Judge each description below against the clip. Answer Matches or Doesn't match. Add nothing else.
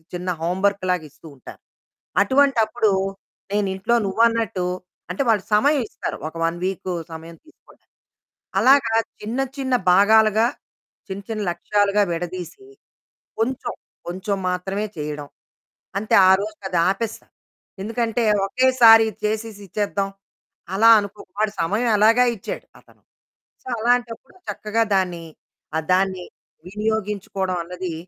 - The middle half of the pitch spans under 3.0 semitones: Doesn't match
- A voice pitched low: Doesn't match